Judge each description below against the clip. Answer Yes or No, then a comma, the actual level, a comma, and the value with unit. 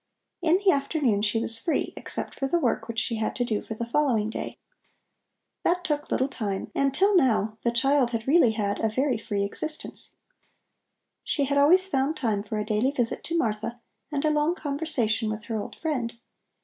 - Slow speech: No, average, 195 wpm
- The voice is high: Yes, high, 245 Hz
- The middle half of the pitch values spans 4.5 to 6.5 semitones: Yes, average, 5.2 semitones